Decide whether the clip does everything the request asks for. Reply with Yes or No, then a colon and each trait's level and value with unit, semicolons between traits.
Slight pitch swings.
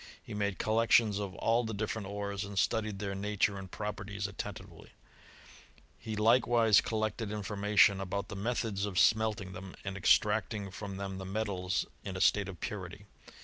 Yes: narrow, 1.9 semitones